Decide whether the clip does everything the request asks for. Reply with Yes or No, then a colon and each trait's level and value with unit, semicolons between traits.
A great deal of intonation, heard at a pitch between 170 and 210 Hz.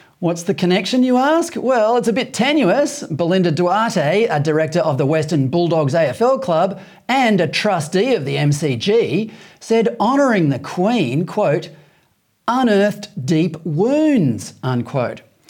Yes: wide, 6.3 semitones; medium, 185 Hz